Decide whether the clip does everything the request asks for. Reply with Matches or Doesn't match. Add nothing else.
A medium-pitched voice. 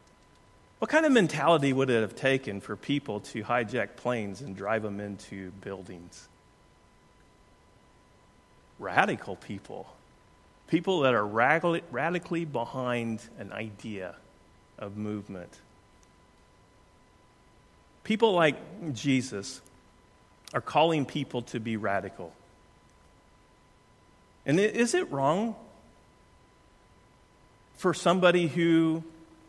Doesn't match